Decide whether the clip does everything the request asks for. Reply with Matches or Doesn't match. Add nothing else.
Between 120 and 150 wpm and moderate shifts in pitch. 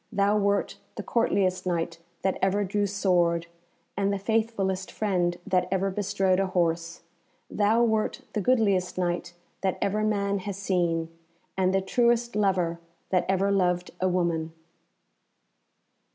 Doesn't match